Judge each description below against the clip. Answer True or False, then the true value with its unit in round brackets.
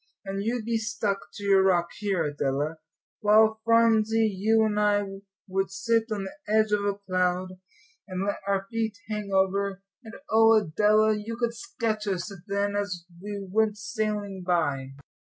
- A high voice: True (205 Hz)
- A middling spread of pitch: False (2.1 semitones)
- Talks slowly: False (160 wpm)